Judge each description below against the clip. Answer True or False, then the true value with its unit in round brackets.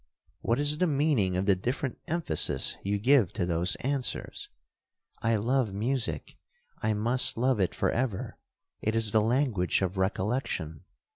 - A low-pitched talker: True (115 Hz)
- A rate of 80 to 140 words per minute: True (135 wpm)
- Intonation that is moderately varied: False (5.8 semitones)